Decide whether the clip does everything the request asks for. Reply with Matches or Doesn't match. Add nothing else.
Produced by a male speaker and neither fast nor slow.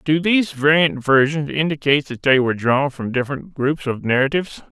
Matches